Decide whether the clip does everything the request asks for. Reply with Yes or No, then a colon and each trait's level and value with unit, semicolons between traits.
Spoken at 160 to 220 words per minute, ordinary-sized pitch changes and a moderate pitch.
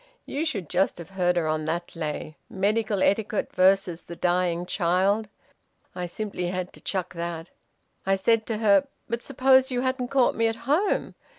No: average, 175 wpm; average, 4.5 semitones; high, 195 Hz